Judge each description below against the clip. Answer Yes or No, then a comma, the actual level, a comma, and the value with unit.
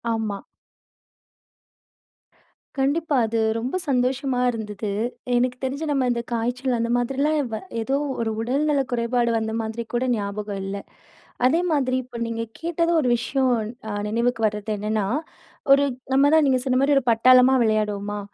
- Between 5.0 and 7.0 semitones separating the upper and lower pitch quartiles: No, average, 3.4 semitones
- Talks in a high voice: Yes, high, 245 Hz